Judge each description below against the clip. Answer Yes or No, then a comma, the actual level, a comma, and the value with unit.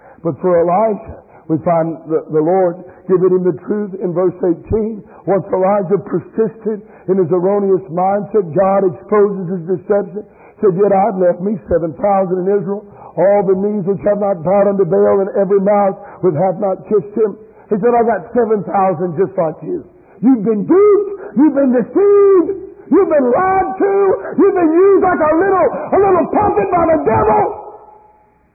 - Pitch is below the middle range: No, high, 205 Hz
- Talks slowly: No, average, 175 wpm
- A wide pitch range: Yes, wide, 7.5 semitones